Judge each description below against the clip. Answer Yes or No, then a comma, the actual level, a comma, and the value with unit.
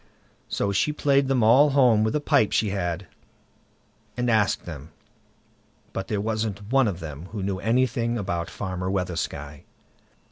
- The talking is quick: No, average, 150 wpm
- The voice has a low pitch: Yes, low, 105 Hz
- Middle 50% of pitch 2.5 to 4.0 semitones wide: No, average, 4.7 semitones